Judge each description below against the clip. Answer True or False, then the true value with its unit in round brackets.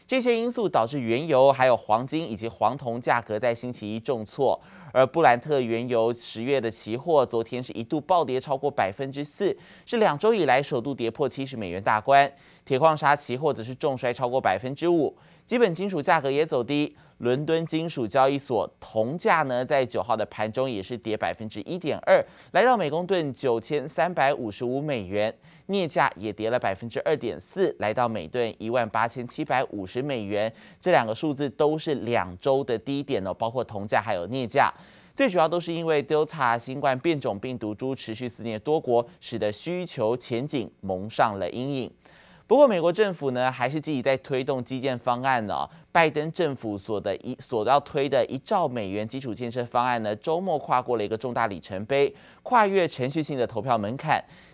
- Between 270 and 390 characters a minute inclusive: True (295 characters per minute)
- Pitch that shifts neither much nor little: True (4.7 semitones)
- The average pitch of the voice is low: True (130 Hz)